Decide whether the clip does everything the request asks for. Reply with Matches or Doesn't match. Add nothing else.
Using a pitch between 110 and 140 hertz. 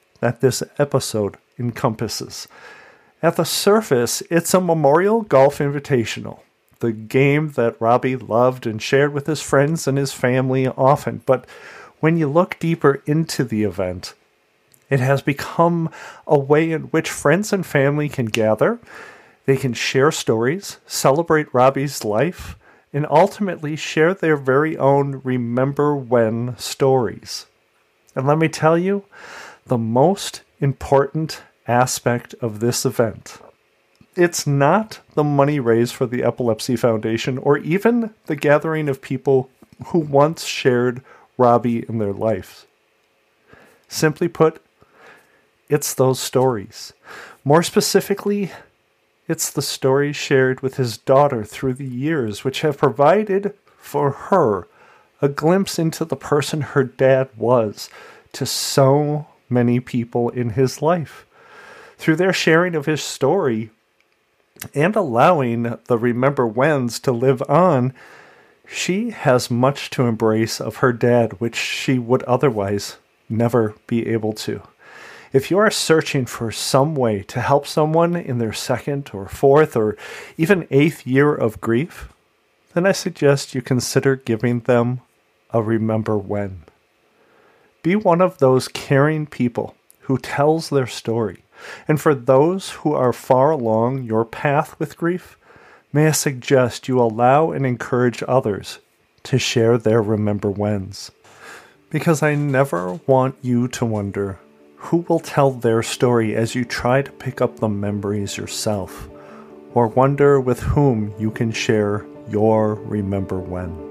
Matches